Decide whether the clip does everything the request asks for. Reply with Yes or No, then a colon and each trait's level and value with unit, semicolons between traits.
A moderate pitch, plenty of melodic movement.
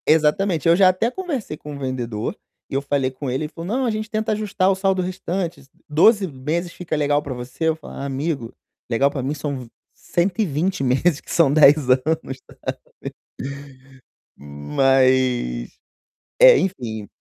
Yes: medium, 150 Hz; wide, 6.0 semitones